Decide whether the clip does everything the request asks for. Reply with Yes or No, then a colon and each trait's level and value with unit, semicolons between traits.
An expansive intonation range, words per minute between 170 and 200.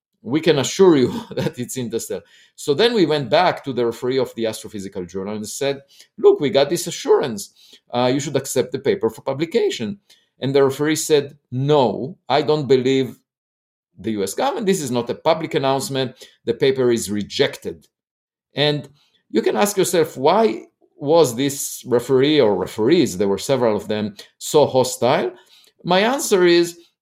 Yes: wide, 5.8 semitones; average, 175 wpm